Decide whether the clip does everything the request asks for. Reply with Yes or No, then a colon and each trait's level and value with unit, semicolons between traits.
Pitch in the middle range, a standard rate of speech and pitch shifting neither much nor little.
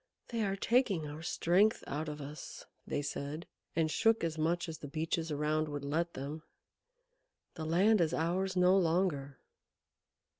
Yes: medium, 160 Hz; average, 155 wpm; average, 3.3 semitones